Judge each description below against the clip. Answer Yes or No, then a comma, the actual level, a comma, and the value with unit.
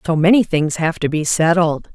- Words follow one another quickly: Yes, fast, 215 wpm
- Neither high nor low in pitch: Yes, medium, 165 Hz